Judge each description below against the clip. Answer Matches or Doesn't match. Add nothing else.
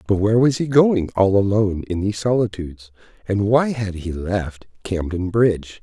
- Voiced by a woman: Doesn't match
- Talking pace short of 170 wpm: Doesn't match